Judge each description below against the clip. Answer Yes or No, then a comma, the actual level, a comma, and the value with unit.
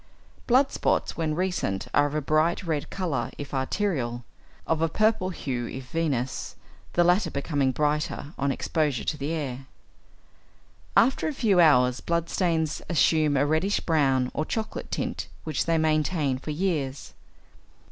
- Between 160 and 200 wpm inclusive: No, average, 150 wpm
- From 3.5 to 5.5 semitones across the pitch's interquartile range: Yes, average, 3.8 semitones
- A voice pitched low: No, medium, 155 Hz